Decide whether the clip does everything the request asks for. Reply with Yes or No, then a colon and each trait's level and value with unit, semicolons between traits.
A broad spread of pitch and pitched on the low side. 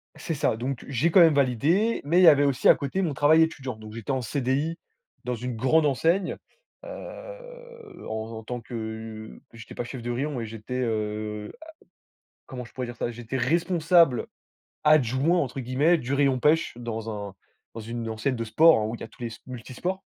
Yes: wide, 5.9 semitones; low, 130 Hz